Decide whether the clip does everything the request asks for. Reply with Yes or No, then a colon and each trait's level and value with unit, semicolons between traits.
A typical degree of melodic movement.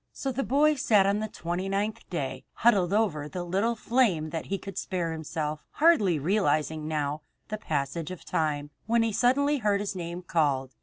No: wide, 5.7 semitones